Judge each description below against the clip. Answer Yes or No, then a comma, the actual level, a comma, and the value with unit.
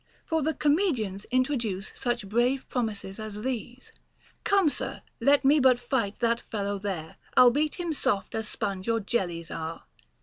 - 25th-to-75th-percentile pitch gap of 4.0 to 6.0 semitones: Yes, average, 4.9 semitones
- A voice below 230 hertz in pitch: No, high, 235 Hz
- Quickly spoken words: No, average, 165 wpm